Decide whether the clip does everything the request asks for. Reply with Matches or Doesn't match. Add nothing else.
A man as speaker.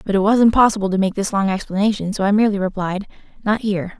Doesn't match